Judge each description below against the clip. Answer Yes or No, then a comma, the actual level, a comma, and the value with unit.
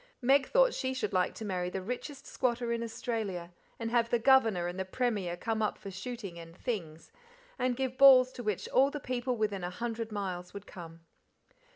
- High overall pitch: Yes, high, 225 Hz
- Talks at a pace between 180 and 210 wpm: Yes, average, 200 wpm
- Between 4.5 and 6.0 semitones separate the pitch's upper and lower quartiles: Yes, average, 5.2 semitones